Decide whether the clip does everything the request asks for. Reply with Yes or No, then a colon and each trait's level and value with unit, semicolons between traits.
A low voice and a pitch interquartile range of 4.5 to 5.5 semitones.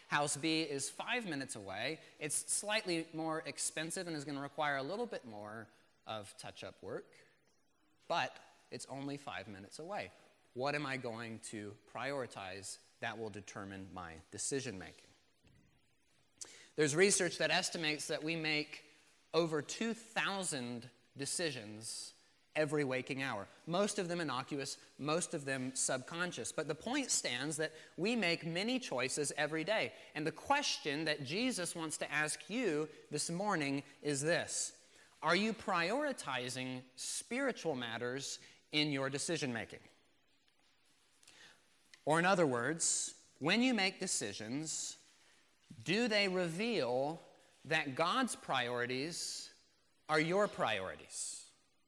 No: medium, 150 Hz; average, 4.8 semitones